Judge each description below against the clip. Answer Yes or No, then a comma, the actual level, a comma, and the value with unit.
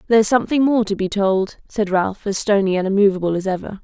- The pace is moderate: No, fast, 220 wpm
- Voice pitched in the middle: No, high, 200 Hz